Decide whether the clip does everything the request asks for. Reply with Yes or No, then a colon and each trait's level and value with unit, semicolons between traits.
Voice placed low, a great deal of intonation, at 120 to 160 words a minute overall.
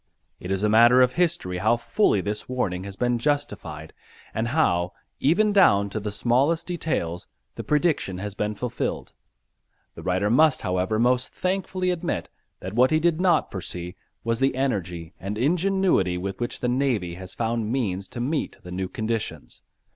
No: low, 115 Hz; wide, 7.3 semitones; average, 170 wpm